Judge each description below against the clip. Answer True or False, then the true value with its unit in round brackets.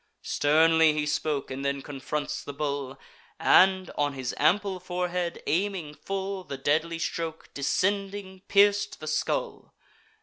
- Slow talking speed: True (130 wpm)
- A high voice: False (160 Hz)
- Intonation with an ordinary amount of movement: True (4.5 semitones)